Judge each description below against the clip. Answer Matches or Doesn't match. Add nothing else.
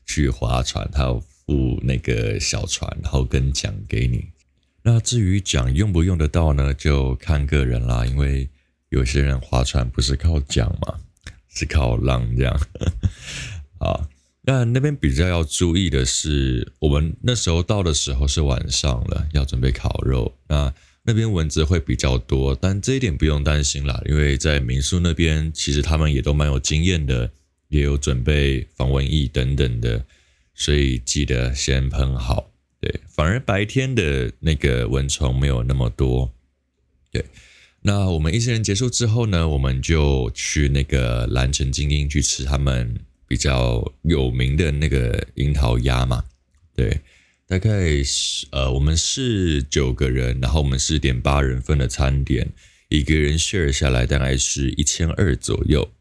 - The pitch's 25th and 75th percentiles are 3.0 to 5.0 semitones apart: Matches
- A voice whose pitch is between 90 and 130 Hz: Doesn't match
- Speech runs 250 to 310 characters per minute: Doesn't match